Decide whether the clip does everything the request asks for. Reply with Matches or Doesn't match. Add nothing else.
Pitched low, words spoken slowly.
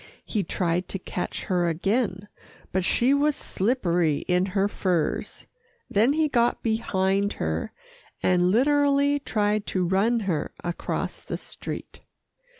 Doesn't match